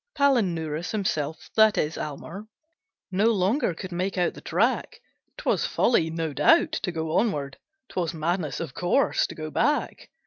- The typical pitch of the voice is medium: Yes, medium, 175 Hz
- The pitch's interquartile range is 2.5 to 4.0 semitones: No, average, 5.3 semitones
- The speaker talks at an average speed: Yes, average, 150 wpm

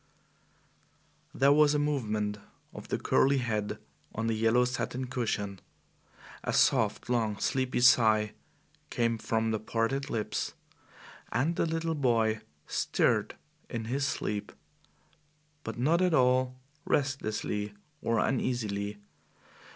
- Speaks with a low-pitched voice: Yes, low, 120 Hz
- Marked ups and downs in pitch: No, average, 3.8 semitones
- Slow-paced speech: Yes, slow, 115 wpm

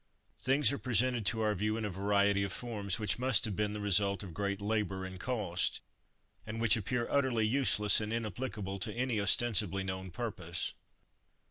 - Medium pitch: No, low, 105 Hz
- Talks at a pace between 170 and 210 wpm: Yes, average, 175 wpm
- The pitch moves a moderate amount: Yes, average, 3.0 semitones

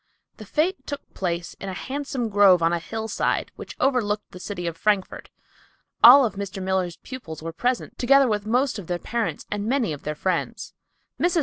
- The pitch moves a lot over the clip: Yes, wide, 5.7 semitones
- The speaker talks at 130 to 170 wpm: No, average, 190 wpm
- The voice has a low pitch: No, high, 205 Hz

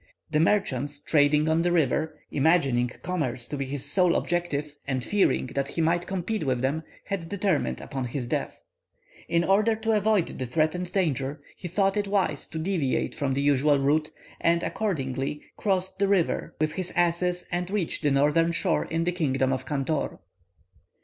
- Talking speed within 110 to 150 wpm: No, average, 175 wpm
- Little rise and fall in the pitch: No, average, 4.5 semitones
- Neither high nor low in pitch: Yes, medium, 160 Hz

